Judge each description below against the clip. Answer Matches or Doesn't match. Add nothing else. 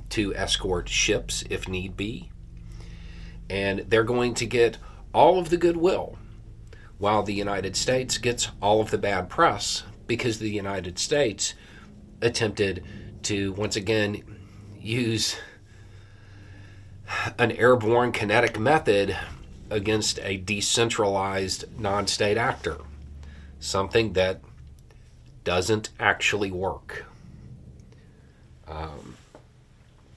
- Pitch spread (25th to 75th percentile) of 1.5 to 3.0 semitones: Matches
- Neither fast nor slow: Doesn't match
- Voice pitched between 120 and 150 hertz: Doesn't match